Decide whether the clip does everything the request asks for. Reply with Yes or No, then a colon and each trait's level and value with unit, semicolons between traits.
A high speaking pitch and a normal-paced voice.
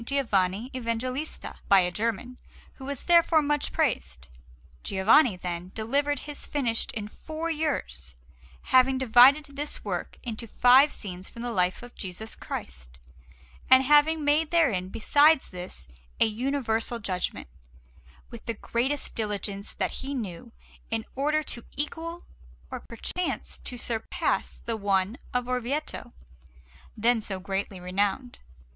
No: high, 235 Hz; slow, 130 wpm